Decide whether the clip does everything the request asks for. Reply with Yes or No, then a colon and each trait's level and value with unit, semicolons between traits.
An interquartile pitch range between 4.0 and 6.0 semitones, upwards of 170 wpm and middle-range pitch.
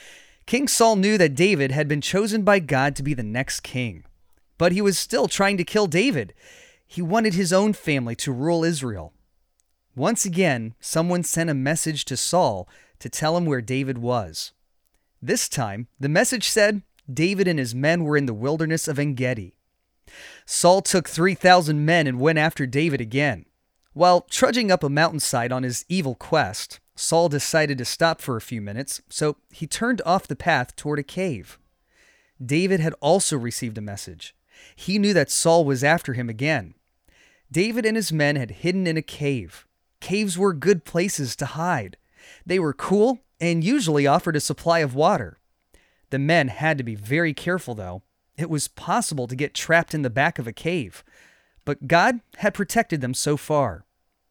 Yes: wide, 5.6 semitones; average, 180 wpm; medium, 155 Hz